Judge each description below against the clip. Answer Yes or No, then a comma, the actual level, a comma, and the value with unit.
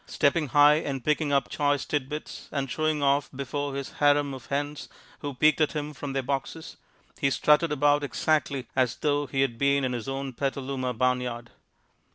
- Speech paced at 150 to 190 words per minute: Yes, average, 180 wpm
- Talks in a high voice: No, medium, 140 Hz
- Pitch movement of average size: No, narrow, 1.6 semitones